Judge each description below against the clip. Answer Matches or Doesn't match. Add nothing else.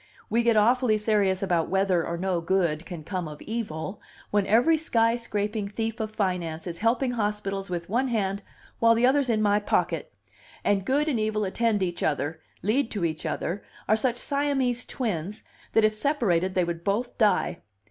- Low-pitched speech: Doesn't match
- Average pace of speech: Matches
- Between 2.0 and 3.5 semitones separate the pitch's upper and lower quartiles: Doesn't match